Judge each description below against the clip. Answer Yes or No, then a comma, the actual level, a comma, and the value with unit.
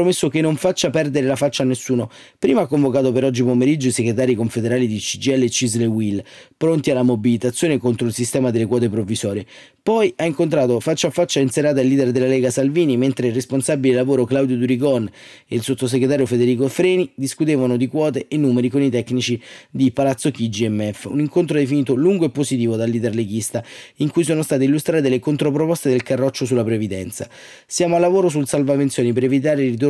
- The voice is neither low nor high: No, low, 130 Hz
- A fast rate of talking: Yes, fast, 195 wpm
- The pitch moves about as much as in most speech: Yes, average, 3.3 semitones